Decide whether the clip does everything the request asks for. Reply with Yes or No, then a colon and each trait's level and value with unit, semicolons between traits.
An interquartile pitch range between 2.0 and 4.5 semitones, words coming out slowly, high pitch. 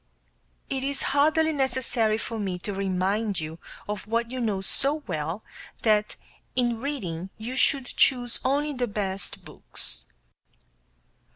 No: average, 5.2 semitones; slow, 130 wpm; high, 230 Hz